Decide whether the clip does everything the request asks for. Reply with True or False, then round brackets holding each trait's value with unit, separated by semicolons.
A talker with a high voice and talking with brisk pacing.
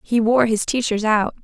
True (225 Hz; 210 wpm)